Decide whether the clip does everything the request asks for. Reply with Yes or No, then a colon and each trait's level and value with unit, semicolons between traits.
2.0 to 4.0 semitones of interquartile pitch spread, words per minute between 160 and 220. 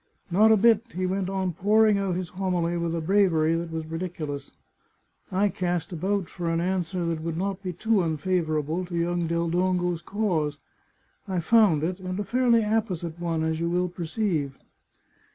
Yes: average, 2.7 semitones; average, 175 wpm